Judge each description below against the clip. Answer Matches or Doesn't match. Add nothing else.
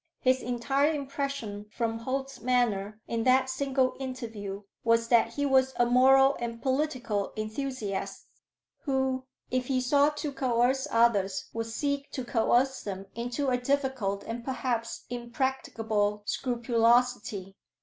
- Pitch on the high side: Matches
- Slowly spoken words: Matches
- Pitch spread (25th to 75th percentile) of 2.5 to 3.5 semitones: Matches